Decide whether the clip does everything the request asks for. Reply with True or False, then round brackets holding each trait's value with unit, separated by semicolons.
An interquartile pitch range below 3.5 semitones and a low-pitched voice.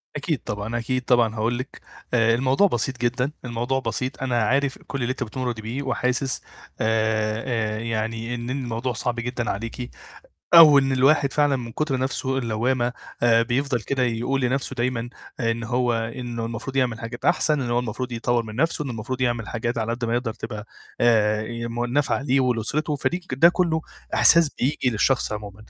True (2.5 semitones; 120 Hz)